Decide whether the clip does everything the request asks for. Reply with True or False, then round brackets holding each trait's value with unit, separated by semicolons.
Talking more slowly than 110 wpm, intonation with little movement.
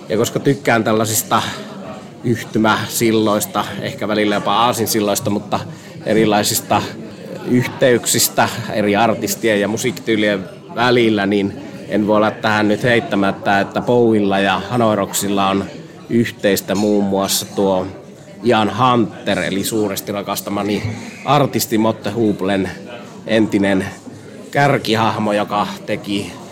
True (100 wpm; 2.0 semitones)